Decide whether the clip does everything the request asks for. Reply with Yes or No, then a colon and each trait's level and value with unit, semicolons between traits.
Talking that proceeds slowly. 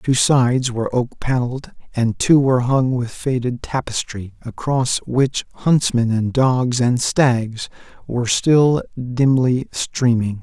Yes: slow, 130 wpm